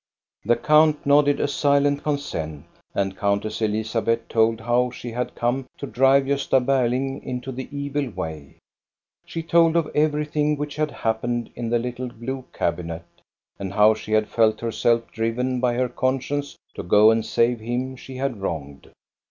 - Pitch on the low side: Yes, low, 125 Hz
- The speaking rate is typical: Yes, average, 165 wpm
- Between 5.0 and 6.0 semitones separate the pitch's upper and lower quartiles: No, average, 4.0 semitones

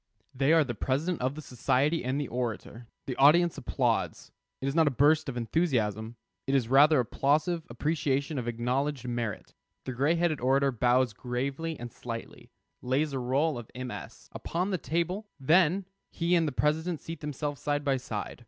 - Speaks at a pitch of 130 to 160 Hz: Yes, medium, 140 Hz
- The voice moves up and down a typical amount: Yes, average, 4.1 semitones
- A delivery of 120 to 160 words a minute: No, average, 175 wpm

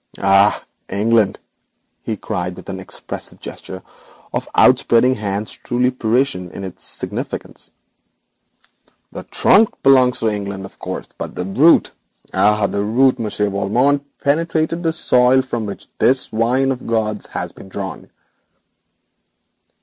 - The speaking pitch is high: No, low, 110 Hz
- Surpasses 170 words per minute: No, slow, 135 wpm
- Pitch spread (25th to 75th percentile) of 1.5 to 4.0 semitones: No, average, 4.6 semitones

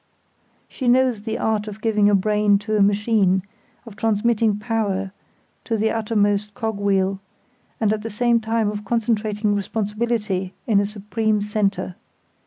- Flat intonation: Yes, narrow, 1.7 semitones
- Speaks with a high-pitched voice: Yes, high, 210 Hz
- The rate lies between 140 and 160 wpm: Yes, average, 150 wpm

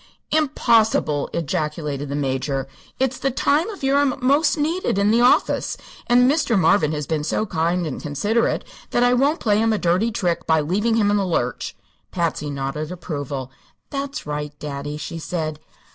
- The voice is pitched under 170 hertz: No, medium, 175 Hz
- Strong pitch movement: Yes, wide, 8.4 semitones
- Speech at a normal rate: Yes, average, 175 wpm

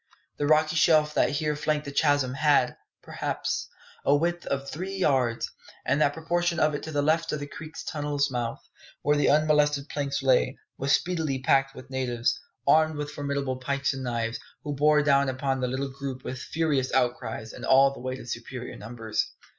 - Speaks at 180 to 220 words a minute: Yes, average, 185 wpm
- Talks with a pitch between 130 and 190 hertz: Yes, medium, 140 Hz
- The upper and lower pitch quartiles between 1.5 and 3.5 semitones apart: Yes, narrow, 2.6 semitones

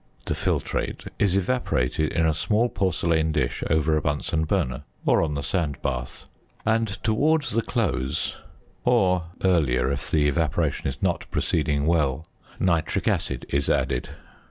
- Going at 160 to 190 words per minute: No, average, 145 wpm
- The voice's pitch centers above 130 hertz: No, very low, 80 Hz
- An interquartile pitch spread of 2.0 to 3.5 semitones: No, average, 4.8 semitones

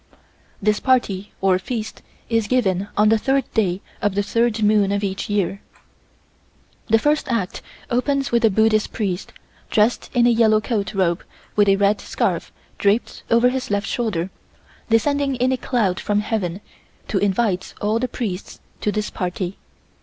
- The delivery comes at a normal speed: Yes, average, 160 wpm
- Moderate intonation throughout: Yes, average, 3.2 semitones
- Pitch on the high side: Yes, high, 215 Hz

